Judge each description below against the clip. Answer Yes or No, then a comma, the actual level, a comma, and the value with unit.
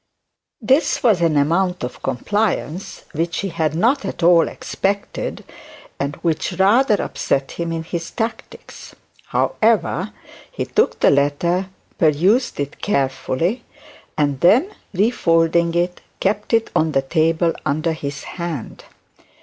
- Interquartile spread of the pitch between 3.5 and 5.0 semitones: Yes, average, 4.5 semitones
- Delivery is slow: Yes, slow, 125 wpm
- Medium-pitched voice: Yes, medium, 170 Hz